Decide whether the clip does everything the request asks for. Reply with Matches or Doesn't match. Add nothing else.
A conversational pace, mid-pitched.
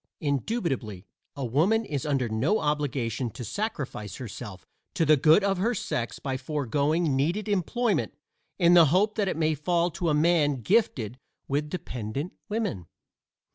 Matches